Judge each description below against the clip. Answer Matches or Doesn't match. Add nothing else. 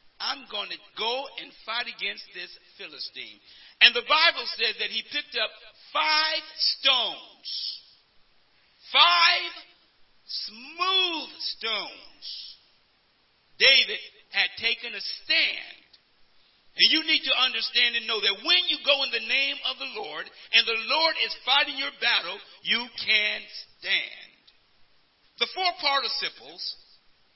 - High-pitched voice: Matches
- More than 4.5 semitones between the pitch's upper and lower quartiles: Matches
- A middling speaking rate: Doesn't match